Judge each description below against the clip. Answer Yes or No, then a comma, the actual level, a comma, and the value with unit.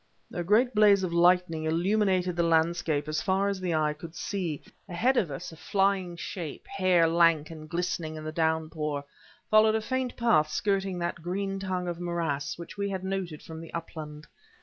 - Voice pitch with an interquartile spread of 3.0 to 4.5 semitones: Yes, average, 3.3 semitones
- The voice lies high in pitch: No, medium, 175 Hz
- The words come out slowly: No, average, 185 wpm